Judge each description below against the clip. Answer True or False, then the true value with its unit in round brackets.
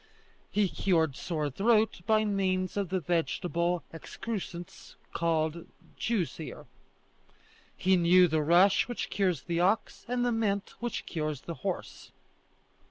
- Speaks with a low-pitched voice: False (180 Hz)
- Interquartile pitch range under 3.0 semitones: False (3.5 semitones)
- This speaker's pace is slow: True (130 wpm)